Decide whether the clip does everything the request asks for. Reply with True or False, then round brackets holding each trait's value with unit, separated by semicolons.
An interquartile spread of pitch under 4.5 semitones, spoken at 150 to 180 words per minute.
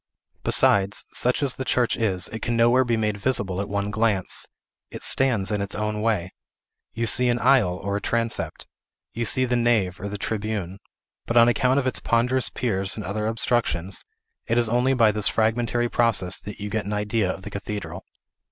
False (3.0 semitones; 195 wpm)